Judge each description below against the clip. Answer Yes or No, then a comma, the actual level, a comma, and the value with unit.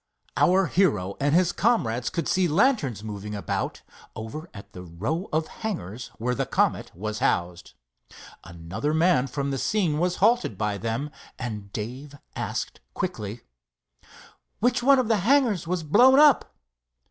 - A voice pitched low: No, medium, 145 Hz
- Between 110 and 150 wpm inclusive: Yes, average, 145 wpm